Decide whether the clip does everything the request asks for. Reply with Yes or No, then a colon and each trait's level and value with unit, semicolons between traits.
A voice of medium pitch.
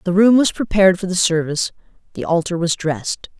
Yes: medium, 180 Hz